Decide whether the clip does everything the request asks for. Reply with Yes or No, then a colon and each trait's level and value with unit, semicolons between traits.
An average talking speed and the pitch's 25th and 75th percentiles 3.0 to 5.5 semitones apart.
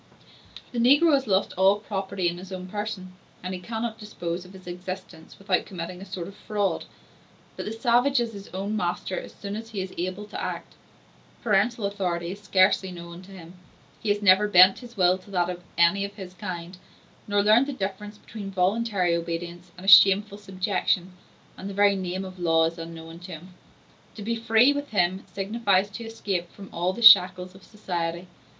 No: average, 195 wpm; narrow, 2.6 semitones